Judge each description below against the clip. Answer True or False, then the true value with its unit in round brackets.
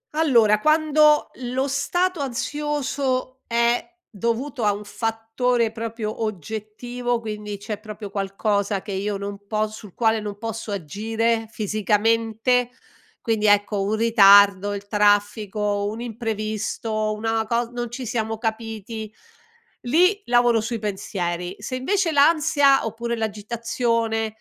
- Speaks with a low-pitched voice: False (225 Hz)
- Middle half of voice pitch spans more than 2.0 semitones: True (2.6 semitones)